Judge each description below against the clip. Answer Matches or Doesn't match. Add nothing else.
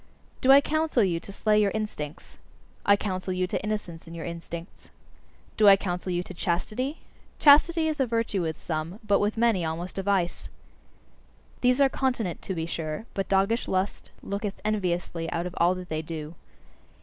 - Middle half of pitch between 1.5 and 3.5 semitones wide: Doesn't match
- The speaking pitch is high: Matches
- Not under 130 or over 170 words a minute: Doesn't match